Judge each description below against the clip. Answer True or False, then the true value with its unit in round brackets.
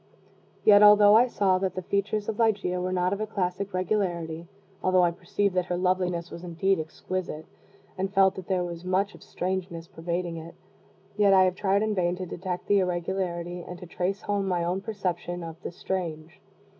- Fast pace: False (195 wpm)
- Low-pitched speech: False (185 Hz)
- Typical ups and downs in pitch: False (2.1 semitones)